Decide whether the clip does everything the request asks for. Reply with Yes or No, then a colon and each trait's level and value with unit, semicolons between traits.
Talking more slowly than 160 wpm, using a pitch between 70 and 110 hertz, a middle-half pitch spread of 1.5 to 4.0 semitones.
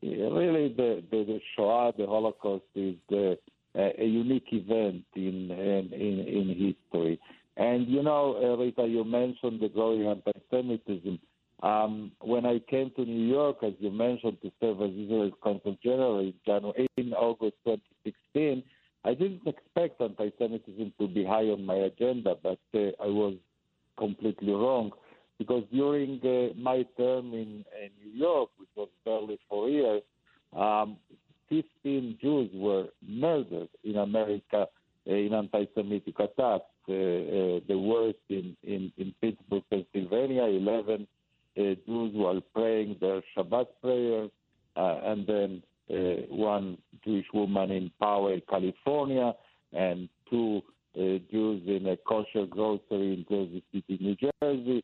Yes: average, 140 wpm; low, 105 Hz; average, 3.4 semitones